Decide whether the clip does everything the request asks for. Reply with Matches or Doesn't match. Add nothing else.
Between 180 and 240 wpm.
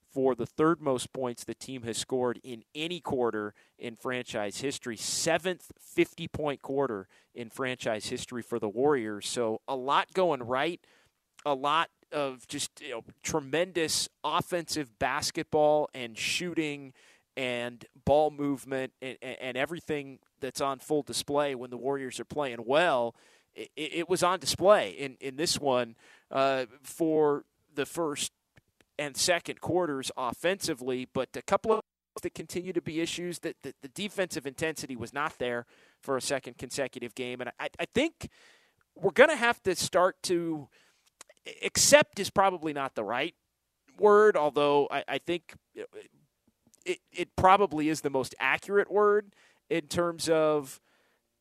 Doesn't match